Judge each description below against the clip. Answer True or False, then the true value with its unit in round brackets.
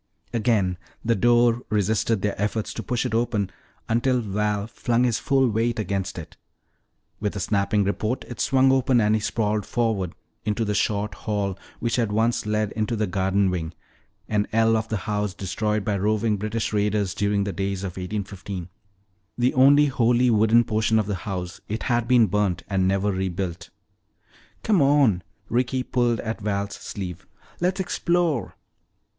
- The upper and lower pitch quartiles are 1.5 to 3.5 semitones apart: True (3.0 semitones)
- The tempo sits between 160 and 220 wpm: True (165 wpm)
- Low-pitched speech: True (105 Hz)